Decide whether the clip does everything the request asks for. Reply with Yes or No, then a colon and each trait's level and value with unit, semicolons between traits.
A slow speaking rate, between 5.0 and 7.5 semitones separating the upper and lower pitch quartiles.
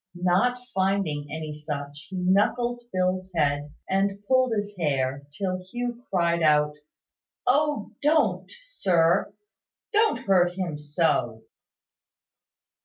Yes: slow, 105 wpm; wide, 5.4 semitones